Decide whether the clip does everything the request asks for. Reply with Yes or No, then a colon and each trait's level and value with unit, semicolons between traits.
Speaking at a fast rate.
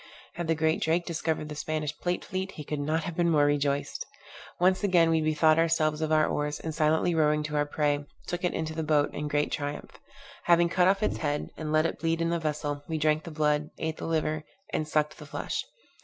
Yes: fast, 230 wpm